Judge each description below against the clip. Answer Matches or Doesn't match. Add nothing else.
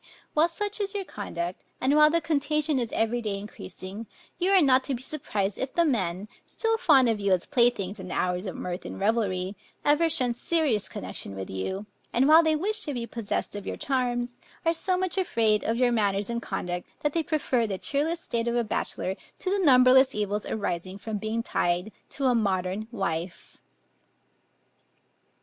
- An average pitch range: Doesn't match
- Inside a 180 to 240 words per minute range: Matches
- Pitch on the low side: Doesn't match